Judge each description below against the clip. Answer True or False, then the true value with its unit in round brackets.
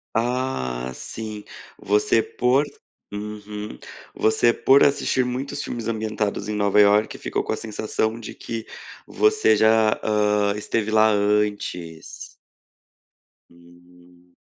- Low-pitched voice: True (105 Hz)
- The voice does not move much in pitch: True (1.8 semitones)